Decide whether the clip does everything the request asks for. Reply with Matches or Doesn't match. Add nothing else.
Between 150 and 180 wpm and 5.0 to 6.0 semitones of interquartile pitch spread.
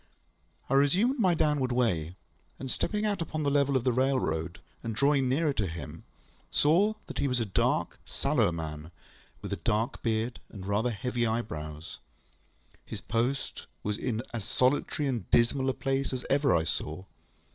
Matches